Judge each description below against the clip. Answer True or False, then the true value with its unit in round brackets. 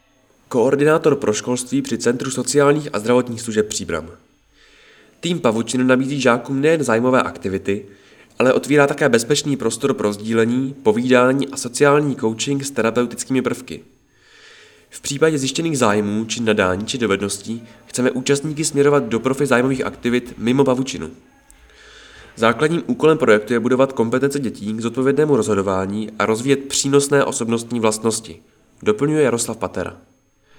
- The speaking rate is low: False (130 wpm)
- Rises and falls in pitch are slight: False (3.8 semitones)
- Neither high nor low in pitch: False (125 Hz)